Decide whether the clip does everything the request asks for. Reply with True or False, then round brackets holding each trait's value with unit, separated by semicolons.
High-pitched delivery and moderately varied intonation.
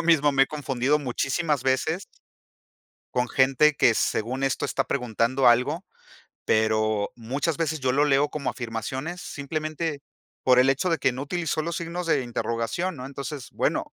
False (135 Hz; 3.8 semitones)